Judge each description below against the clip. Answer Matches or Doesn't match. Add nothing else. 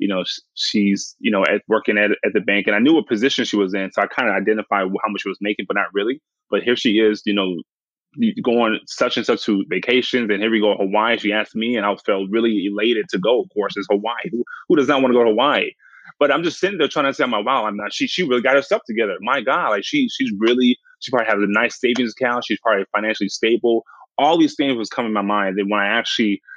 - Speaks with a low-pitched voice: Matches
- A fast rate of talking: Matches